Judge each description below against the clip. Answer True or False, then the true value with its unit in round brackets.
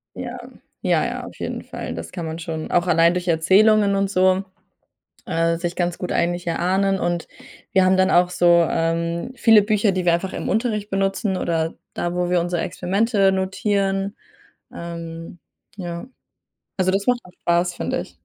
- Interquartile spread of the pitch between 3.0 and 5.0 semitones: False (2.4 semitones)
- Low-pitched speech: False (180 Hz)